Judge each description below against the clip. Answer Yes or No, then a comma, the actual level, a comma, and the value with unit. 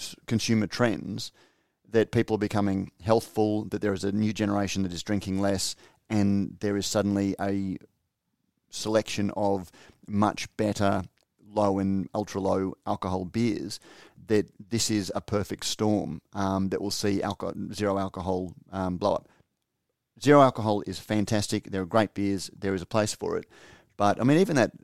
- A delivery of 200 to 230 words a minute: No, average, 160 wpm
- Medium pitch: No, low, 100 Hz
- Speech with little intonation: Yes, narrow, 1.7 semitones